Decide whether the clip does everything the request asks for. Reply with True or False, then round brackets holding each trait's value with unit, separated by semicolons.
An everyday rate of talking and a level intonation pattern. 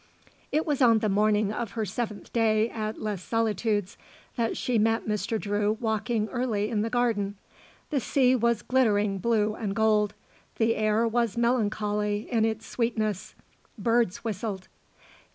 True (150 wpm; 2.0 semitones)